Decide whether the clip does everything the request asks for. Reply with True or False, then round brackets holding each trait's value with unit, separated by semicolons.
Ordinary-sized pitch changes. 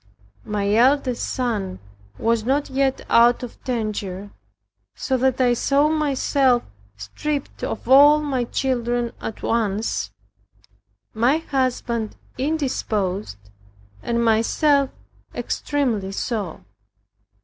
True (4.0 semitones)